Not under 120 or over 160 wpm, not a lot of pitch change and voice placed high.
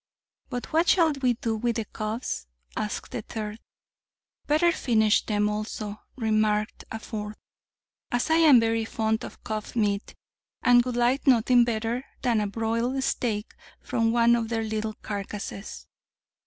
Yes: average, 150 wpm; narrow, 2.2 semitones; high, 225 Hz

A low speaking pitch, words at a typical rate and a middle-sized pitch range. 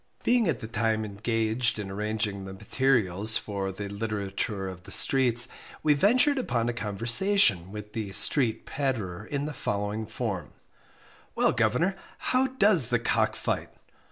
Yes: low, 110 Hz; average, 150 wpm; average, 5.0 semitones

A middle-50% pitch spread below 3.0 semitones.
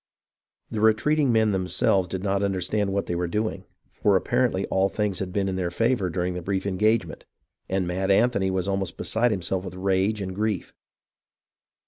Yes: narrow, 2.6 semitones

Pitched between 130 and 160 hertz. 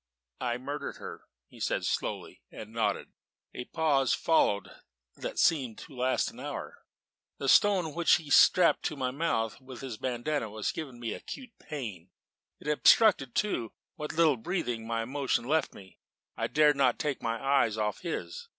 Yes: low, 135 Hz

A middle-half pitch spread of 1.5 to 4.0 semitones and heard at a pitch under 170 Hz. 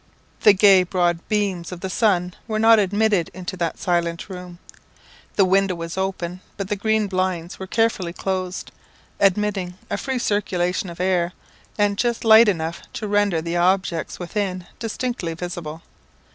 No: average, 2.9 semitones; medium, 185 Hz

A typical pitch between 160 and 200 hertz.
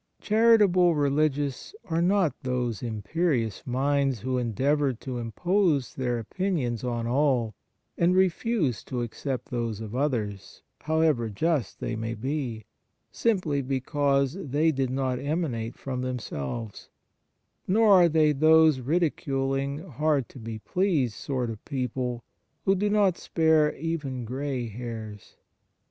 No: low, 135 Hz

